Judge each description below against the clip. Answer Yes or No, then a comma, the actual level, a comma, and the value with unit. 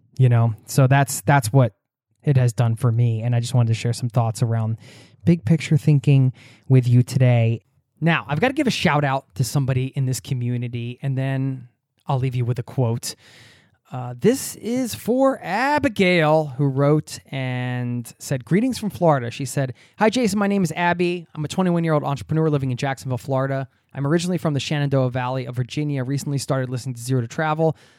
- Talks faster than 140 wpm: Yes, average, 195 wpm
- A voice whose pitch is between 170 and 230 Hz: No, low, 135 Hz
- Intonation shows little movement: No, average, 3.8 semitones